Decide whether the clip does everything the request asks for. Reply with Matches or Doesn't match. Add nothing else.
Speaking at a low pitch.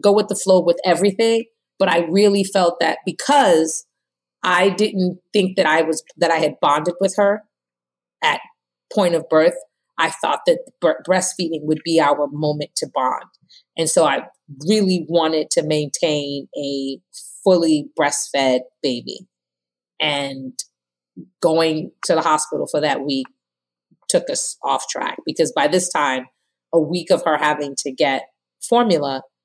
Doesn't match